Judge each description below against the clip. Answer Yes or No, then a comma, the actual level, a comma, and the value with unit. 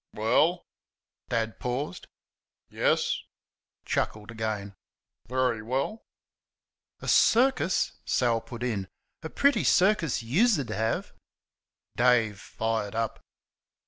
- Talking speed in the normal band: No, slow, 90 wpm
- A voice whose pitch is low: Yes, low, 120 Hz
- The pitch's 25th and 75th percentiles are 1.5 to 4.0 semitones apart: No, average, 5.3 semitones